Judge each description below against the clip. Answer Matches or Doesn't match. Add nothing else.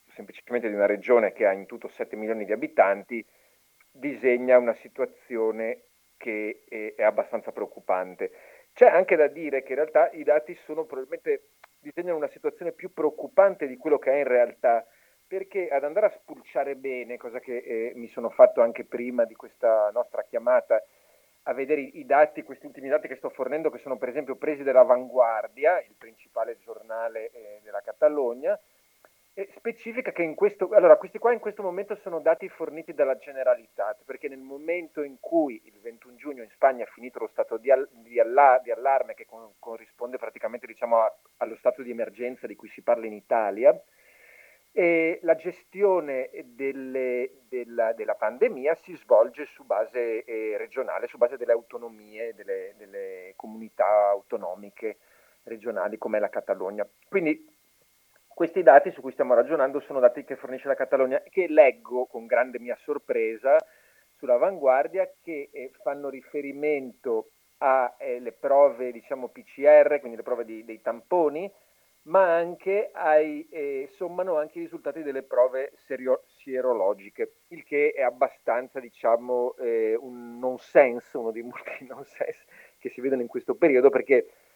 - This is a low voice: Doesn't match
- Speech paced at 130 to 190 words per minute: Matches